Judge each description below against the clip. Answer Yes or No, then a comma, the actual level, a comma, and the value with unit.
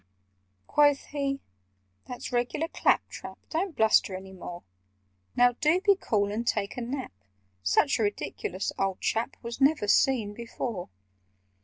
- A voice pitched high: Yes, high, 235 Hz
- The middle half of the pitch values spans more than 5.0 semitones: Yes, wide, 5.5 semitones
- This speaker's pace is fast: No, average, 140 wpm